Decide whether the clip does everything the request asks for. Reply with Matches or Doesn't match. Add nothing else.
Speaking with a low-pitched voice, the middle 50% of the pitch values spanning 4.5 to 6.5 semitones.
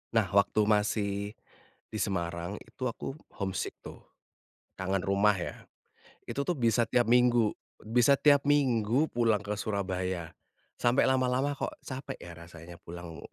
Matches